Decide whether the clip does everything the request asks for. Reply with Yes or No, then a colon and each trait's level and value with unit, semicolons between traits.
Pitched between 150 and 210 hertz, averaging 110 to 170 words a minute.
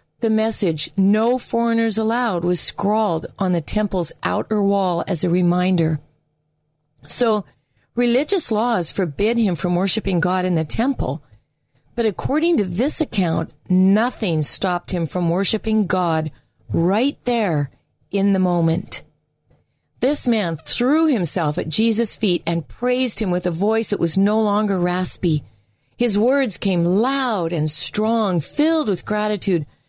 Yes: high, 190 Hz; average, 140 wpm